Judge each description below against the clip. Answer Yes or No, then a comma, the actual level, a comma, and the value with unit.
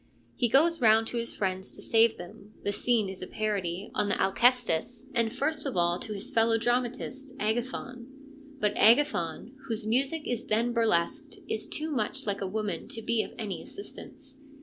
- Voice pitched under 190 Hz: No, high, 225 Hz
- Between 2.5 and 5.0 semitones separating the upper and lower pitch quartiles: Yes, average, 3.7 semitones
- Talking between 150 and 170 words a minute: No, average, 180 wpm